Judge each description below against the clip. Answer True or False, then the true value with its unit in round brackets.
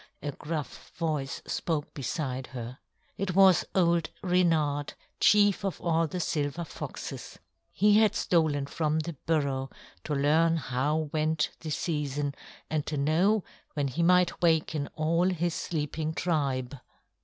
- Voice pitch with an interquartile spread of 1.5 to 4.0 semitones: True (2.9 semitones)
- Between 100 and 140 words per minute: True (135 wpm)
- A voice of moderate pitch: True (155 Hz)